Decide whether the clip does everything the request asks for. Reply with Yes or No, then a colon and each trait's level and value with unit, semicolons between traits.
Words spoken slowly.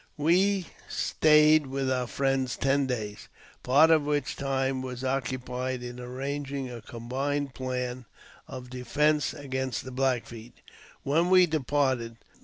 Yes: slow, 130 wpm